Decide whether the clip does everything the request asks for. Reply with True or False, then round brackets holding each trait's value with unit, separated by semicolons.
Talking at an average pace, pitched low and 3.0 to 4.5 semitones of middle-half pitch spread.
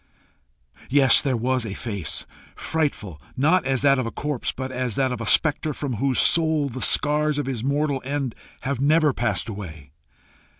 True (175 wpm; 130 Hz; 3.8 semitones)